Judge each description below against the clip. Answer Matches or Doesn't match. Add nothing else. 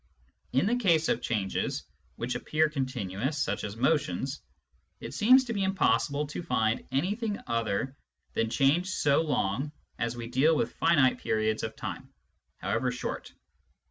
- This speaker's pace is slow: Doesn't match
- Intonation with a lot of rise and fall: Matches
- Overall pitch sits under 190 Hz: Matches